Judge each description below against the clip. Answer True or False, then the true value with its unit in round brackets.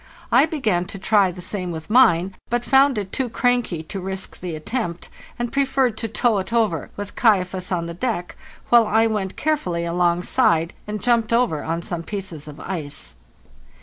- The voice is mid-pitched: False (195 Hz)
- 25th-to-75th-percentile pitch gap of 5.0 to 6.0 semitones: True (5.3 semitones)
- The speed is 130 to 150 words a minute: False (180 wpm)